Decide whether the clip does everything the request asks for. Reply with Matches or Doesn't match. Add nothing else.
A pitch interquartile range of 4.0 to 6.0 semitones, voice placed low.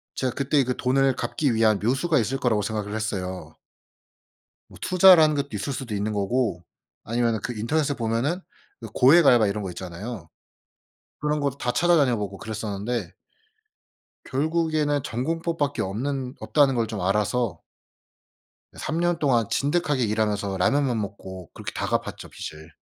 Matches